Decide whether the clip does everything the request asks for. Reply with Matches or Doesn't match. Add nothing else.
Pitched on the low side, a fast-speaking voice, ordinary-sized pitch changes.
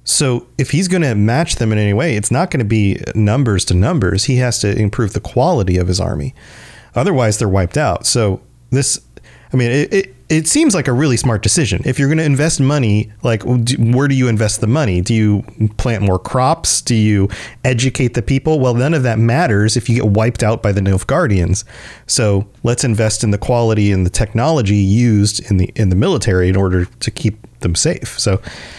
Matches